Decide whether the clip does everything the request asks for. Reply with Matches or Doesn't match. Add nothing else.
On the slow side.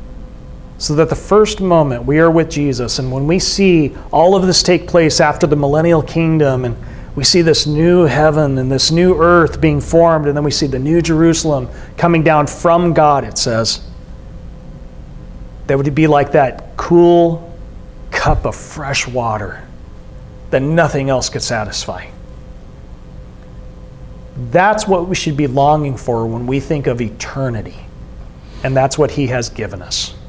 Doesn't match